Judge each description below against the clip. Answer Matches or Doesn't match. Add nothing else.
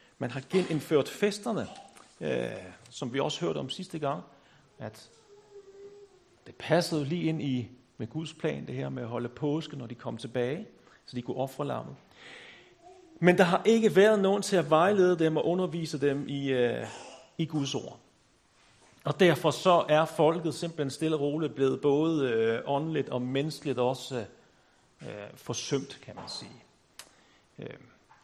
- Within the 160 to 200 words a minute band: Doesn't match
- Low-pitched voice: Doesn't match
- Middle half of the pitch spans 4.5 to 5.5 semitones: Matches